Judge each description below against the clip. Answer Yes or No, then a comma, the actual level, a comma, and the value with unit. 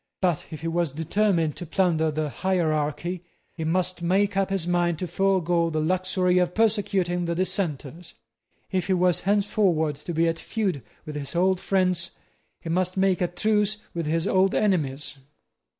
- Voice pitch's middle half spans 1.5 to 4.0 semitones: Yes, average, 2.7 semitones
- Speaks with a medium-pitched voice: Yes, medium, 175 Hz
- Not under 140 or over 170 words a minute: Yes, average, 165 wpm